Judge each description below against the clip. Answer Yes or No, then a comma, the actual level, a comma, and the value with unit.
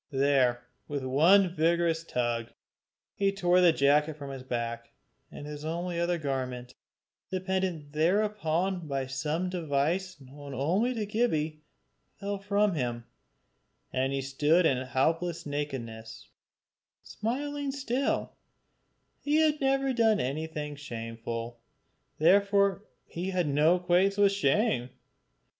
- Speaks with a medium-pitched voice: Yes, medium, 160 Hz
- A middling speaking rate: No, slow, 115 wpm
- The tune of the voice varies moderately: No, wide, 6.2 semitones